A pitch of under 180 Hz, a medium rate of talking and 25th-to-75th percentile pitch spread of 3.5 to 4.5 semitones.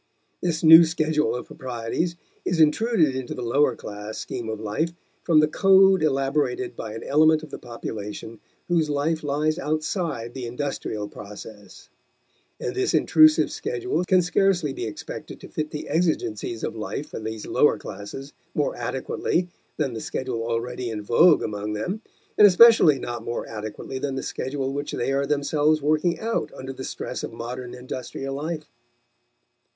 No: medium, 140 Hz; average, 160 wpm; wide, 5.4 semitones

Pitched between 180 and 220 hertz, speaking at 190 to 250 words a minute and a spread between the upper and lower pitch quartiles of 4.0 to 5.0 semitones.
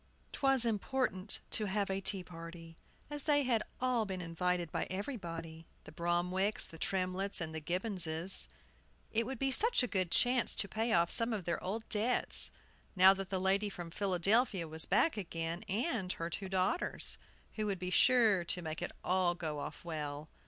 No: high, 190 Hz; average, 180 wpm; average, 4.4 semitones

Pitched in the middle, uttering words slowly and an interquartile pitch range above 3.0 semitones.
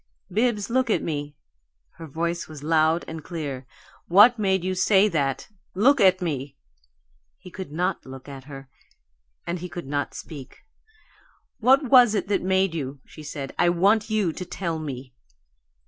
No: medium, 170 Hz; average, 160 wpm; average, 5.2 semitones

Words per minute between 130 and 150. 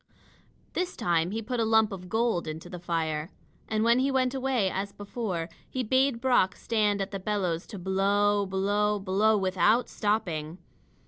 No: average, 170 wpm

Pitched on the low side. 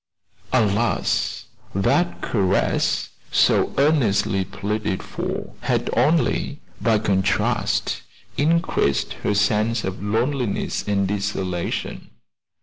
Yes: low, 105 Hz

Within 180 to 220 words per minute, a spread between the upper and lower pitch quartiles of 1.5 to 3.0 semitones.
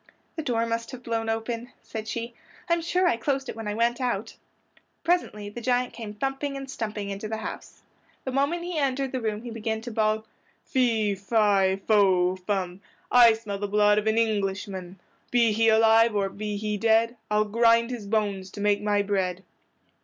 Yes: average, 190 wpm; narrow, 2.6 semitones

